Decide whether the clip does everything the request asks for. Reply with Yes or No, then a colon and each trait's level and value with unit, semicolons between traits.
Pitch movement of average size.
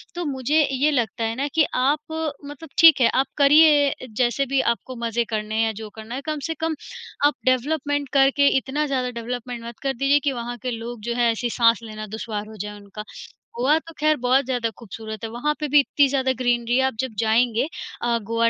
Yes: average, 3.6 semitones